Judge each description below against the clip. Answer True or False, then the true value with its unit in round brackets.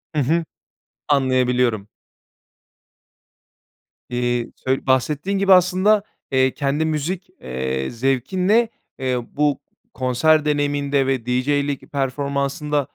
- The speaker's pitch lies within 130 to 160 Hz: True (140 Hz)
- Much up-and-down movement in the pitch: False (3.3 semitones)